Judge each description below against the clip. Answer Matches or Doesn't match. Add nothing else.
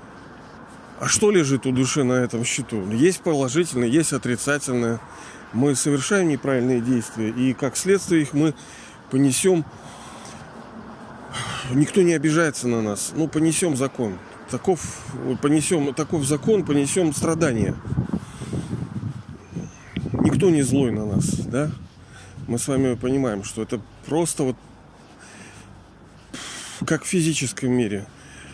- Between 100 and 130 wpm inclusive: Matches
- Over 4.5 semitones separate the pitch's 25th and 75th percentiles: Matches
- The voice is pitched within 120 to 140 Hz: Matches